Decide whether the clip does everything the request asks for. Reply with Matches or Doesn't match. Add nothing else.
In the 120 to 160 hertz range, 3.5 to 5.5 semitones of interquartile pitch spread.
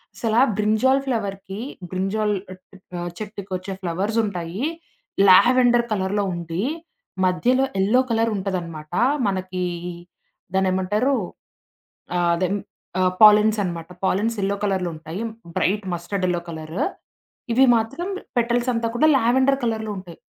Doesn't match